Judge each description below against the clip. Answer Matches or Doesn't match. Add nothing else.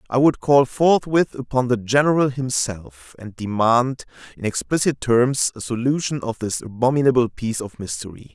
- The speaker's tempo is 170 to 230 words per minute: Doesn't match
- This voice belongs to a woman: Doesn't match